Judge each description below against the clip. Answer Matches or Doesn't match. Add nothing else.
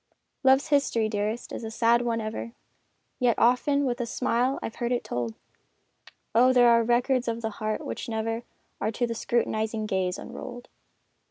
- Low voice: Doesn't match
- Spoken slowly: Doesn't match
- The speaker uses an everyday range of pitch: Doesn't match